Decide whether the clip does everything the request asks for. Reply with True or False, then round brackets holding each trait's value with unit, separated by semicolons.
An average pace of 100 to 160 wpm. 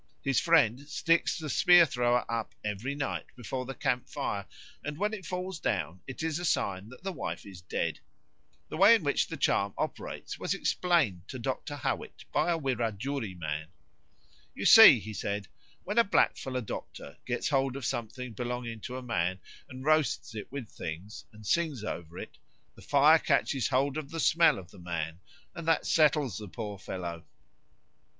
False (180 wpm)